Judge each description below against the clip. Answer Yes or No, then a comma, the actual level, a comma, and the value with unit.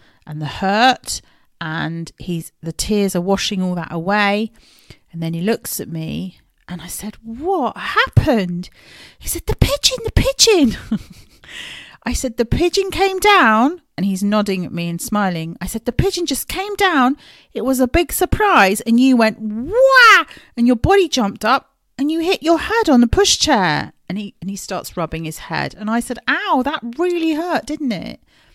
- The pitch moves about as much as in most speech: No, wide, 9.0 semitones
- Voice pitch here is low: No, high, 235 Hz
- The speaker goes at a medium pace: Yes, average, 185 wpm